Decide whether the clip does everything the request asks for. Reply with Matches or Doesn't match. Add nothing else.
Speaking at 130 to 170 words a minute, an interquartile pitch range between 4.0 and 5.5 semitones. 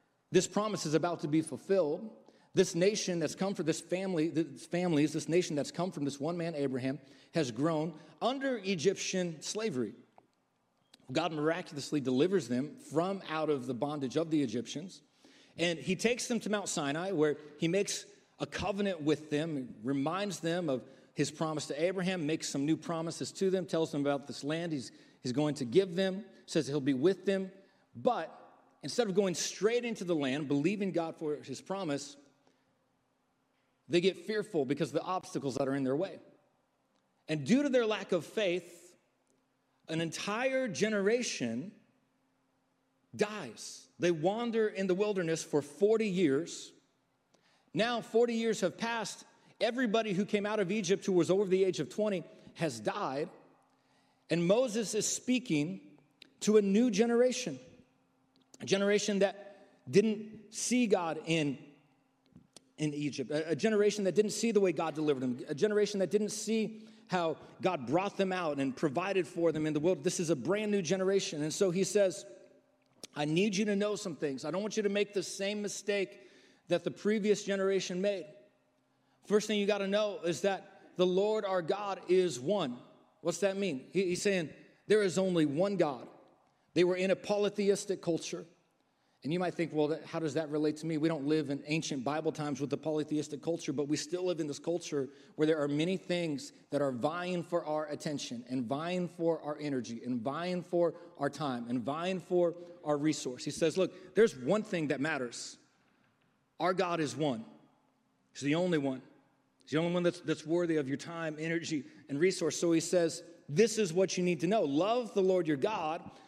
Doesn't match